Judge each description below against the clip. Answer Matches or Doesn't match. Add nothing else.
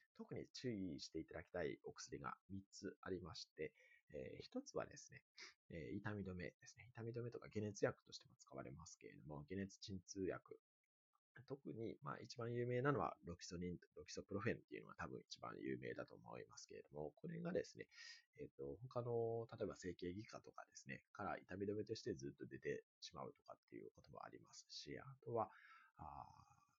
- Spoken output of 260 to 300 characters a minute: Doesn't match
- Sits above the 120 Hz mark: Doesn't match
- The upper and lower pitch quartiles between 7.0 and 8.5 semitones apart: Matches